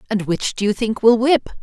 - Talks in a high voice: Yes, high, 225 Hz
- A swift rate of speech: Yes, fast, 260 wpm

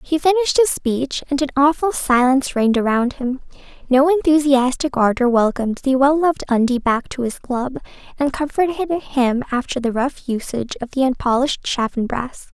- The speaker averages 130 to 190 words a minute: Yes, average, 160 wpm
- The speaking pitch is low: No, very high, 270 Hz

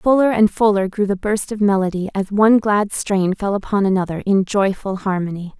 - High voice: Yes, high, 200 Hz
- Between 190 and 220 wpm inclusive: Yes, average, 195 wpm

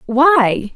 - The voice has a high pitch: Yes, very high, 260 Hz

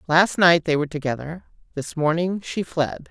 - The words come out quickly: No, average, 175 wpm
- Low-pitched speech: No, medium, 160 Hz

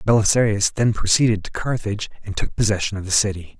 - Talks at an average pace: Yes, average, 185 wpm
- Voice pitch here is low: Yes, low, 105 Hz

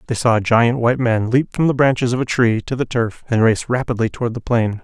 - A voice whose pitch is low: Yes, low, 120 Hz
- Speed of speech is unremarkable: No, fast, 275 wpm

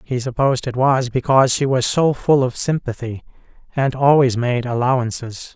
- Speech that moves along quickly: No, average, 160 wpm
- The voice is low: Yes, low, 130 Hz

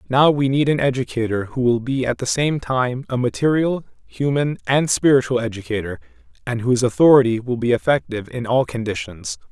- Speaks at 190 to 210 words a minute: No, average, 170 wpm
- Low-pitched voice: Yes, low, 125 Hz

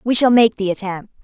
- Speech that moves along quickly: Yes, fast, 240 wpm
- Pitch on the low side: No, high, 210 Hz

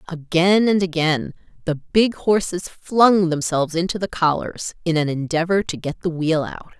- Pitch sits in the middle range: Yes, medium, 170 Hz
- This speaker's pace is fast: No, average, 170 wpm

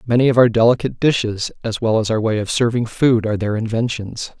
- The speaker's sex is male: Yes, male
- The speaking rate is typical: No, fast, 220 wpm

